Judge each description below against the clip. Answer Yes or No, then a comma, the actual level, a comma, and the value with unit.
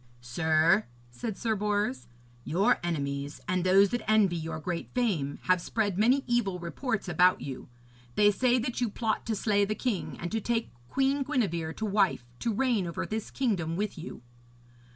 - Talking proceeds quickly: No, average, 175 wpm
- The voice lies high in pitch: Yes, high, 200 Hz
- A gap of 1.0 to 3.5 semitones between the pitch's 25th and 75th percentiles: No, average, 4.9 semitones